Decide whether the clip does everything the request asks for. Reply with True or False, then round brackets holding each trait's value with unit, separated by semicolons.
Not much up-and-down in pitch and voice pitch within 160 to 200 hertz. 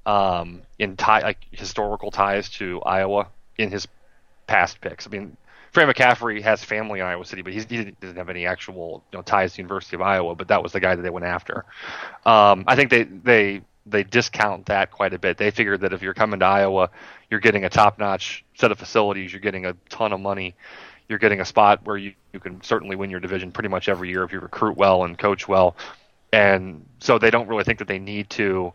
False (2.1 semitones; 100 Hz)